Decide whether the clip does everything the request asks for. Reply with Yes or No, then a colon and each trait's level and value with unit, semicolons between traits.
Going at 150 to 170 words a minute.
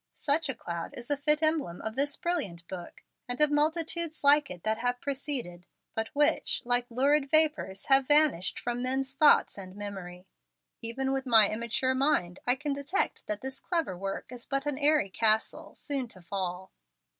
No: average, 180 wpm